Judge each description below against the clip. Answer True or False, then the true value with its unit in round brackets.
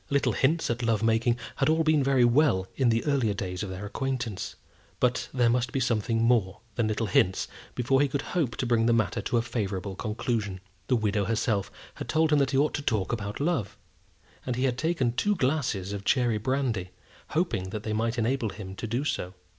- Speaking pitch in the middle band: False (120 Hz)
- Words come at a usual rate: False (210 wpm)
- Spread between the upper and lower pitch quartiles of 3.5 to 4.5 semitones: True (4.1 semitones)